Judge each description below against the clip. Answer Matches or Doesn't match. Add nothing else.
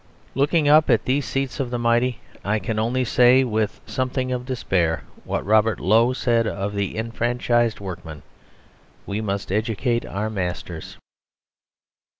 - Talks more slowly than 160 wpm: Matches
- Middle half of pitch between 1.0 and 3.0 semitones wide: Doesn't match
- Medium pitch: Doesn't match